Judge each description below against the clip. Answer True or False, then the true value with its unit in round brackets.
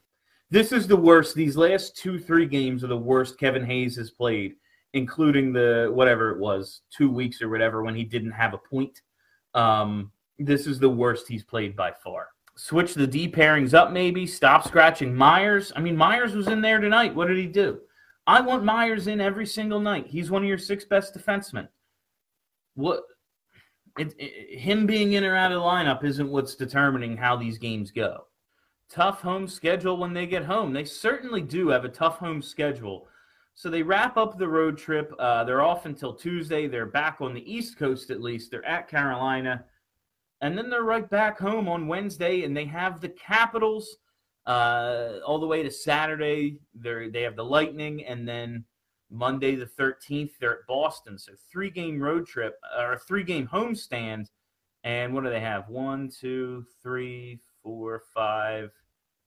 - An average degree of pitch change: False (7.0 semitones)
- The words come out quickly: False (185 wpm)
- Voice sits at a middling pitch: True (145 Hz)